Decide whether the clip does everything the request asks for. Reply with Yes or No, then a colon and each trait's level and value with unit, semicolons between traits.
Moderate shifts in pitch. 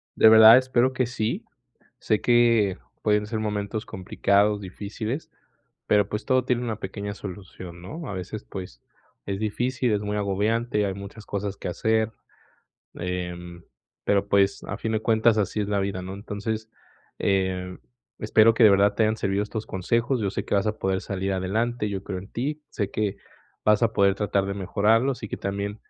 No: narrow, 2.2 semitones